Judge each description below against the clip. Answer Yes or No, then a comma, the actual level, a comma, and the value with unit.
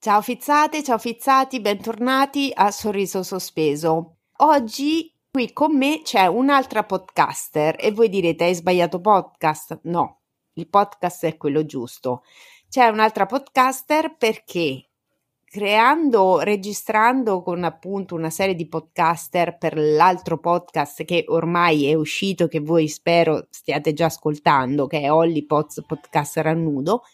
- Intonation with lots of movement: Yes, wide, 5.9 semitones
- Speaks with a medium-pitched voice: Yes, medium, 180 Hz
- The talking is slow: No, average, 130 wpm